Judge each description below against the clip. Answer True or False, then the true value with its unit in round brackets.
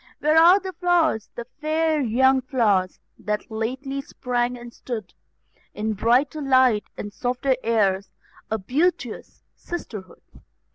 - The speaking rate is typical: False (125 wpm)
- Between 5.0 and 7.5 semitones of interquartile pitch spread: True (5.4 semitones)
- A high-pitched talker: True (250 Hz)